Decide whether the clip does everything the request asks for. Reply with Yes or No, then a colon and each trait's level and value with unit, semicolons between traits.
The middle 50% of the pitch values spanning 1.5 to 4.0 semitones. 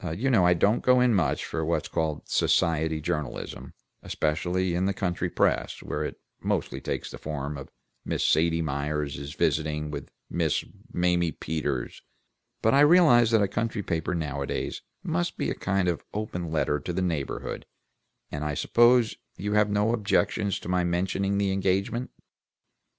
No: average, 4.9 semitones